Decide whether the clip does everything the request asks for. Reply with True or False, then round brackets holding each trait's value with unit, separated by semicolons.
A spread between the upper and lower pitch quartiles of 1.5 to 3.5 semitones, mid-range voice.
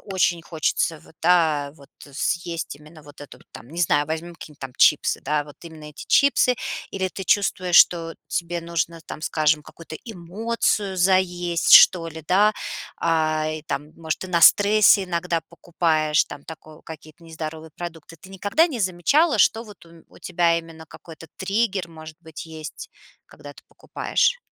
True (2.8 semitones; 165 Hz)